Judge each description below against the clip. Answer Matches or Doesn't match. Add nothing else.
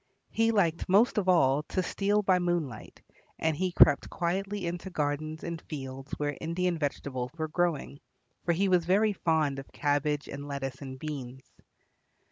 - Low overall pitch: Doesn't match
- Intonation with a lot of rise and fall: Doesn't match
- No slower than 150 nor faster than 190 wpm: Matches